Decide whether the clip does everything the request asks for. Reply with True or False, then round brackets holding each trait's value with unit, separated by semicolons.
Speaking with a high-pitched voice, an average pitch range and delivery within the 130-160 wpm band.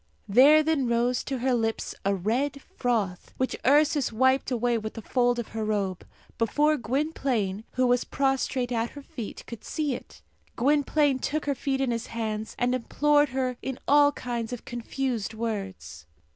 False (245 Hz; 3.3 semitones; 170 wpm)